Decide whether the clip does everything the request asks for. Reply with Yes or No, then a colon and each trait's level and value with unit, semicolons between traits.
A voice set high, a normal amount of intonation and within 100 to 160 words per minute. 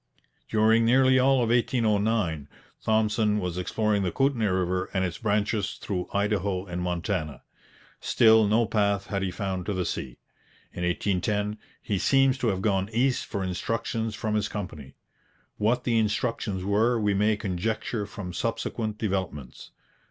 No: low, 105 Hz; average, 3.1 semitones; average, 150 wpm